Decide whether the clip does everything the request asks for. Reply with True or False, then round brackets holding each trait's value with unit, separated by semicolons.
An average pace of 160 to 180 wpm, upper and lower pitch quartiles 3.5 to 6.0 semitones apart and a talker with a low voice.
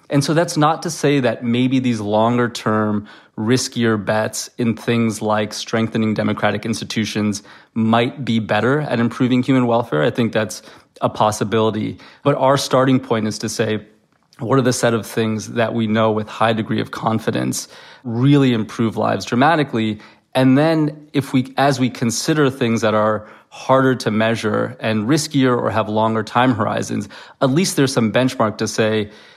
False (170 wpm; 3.0 semitones; 115 Hz)